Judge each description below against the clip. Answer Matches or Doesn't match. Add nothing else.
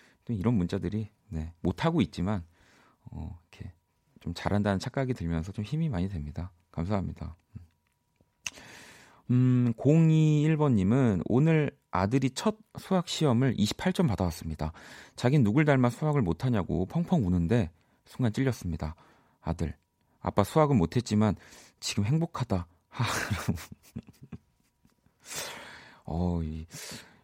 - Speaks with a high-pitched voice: Doesn't match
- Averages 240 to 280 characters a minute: Matches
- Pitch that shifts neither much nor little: Doesn't match